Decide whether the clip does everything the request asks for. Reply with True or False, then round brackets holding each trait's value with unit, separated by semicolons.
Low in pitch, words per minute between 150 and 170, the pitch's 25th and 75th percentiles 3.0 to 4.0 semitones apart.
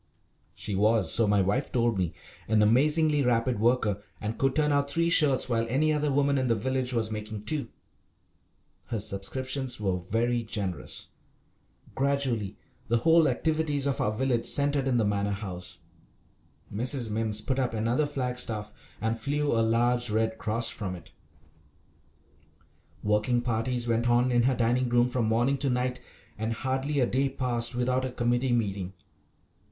True (120 Hz; 160 wpm; 3.3 semitones)